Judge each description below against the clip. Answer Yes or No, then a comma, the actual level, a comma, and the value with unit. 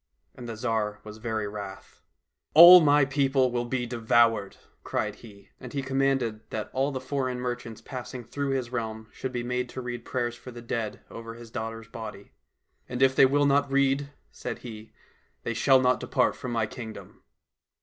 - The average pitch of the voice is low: Yes, low, 120 Hz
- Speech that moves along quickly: No, average, 190 wpm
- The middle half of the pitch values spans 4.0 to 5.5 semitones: No, average, 2.9 semitones